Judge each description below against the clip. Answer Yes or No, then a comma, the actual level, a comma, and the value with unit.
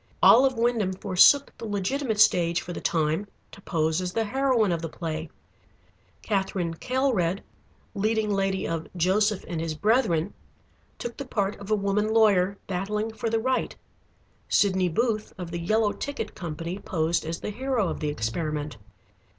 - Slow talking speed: No, average, 160 wpm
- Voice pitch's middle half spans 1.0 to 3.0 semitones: No, average, 4.5 semitones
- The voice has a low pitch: No, high, 195 Hz